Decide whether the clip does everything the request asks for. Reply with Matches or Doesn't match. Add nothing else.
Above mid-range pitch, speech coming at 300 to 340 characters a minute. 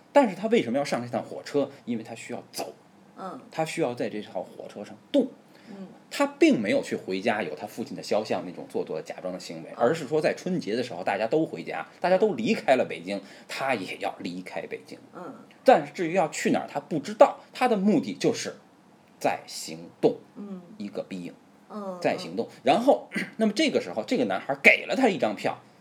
Matches